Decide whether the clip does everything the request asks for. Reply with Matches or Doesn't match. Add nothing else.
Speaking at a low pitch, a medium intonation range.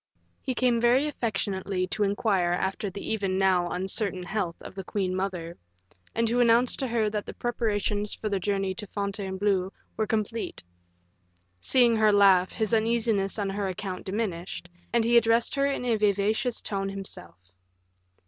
Doesn't match